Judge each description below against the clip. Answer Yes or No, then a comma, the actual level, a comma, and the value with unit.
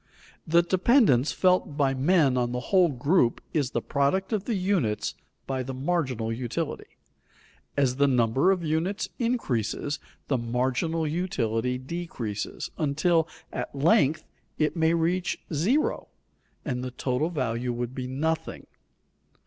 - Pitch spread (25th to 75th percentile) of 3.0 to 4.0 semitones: No, average, 5.3 semitones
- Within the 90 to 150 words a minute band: Yes, slow, 135 wpm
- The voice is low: No, medium, 145 Hz